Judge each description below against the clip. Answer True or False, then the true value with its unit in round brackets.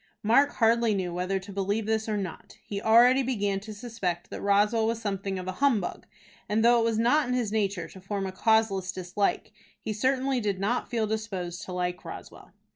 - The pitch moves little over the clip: False (3.0 semitones)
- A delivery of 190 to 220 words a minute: True (200 wpm)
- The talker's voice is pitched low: False (210 Hz)